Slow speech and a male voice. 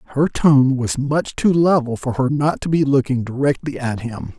No: fast, 205 wpm; male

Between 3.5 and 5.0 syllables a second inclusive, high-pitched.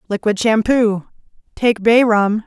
Yes: 4.7 syllables/s; high, 215 Hz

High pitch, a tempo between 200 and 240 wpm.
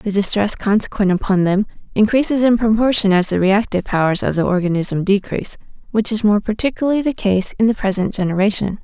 No: high, 205 Hz; average, 175 wpm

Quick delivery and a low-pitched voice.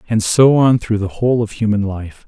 Yes: fast, 240 wpm; low, 110 Hz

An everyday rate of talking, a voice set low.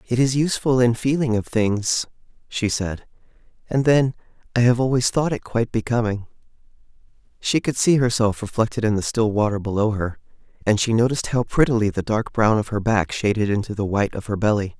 Yes: average, 190 wpm; low, 110 Hz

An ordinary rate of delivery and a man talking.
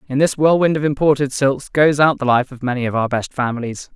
No: fast, 245 wpm; male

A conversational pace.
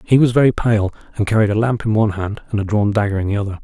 No: fast, 295 wpm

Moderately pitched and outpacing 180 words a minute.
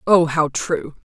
No: medium, 160 Hz; average, 160 wpm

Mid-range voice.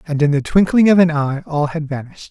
Yes: medium, 155 Hz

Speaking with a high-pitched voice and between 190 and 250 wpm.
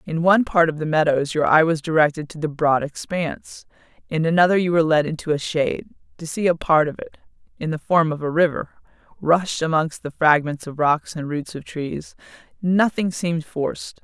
No: medium, 160 Hz; average, 200 wpm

